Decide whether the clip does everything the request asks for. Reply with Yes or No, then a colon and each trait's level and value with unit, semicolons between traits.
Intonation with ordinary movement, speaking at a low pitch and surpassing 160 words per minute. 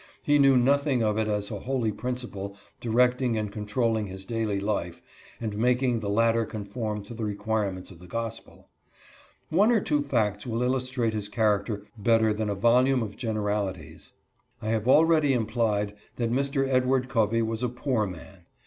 Yes: average, 3.3 semitones; low, 115 Hz; average, 170 wpm